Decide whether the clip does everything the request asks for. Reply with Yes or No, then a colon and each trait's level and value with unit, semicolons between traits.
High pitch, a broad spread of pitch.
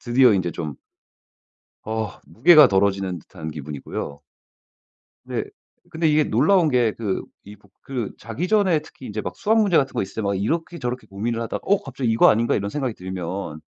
No: low, 115 Hz; wide, 7.3 semitones